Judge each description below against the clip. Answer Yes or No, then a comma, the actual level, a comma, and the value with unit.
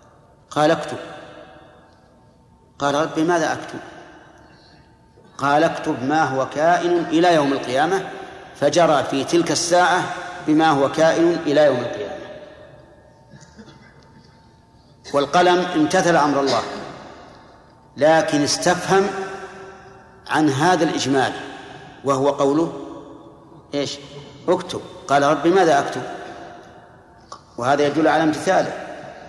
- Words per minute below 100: Yes, average, 90 wpm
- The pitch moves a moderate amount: Yes, average, 3.9 semitones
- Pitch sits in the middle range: Yes, medium, 160 Hz